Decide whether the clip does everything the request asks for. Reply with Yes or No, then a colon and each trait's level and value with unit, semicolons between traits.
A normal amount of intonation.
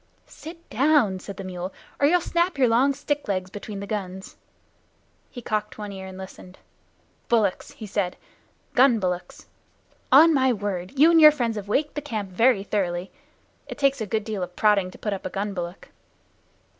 No: wide, 6.1 semitones